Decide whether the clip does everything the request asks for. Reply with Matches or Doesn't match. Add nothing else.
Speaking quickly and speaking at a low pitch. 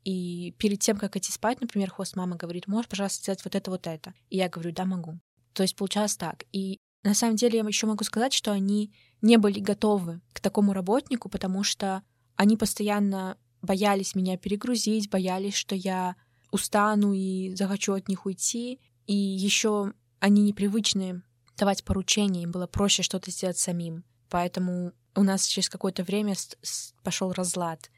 Doesn't match